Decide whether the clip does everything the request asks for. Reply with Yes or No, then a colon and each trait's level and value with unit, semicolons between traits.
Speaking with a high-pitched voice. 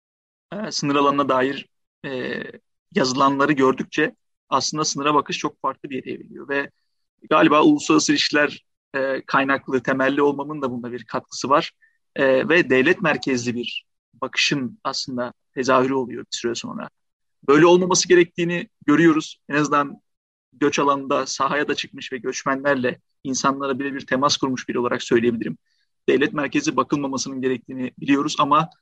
No: medium, 140 Hz